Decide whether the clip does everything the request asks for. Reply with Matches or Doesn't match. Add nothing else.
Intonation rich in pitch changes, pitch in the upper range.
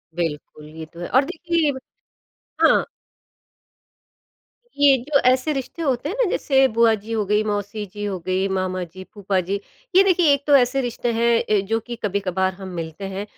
Matches